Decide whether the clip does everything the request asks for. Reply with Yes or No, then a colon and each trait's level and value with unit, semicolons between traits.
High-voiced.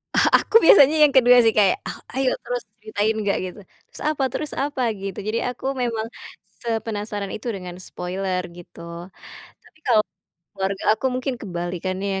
Yes: high, 215 Hz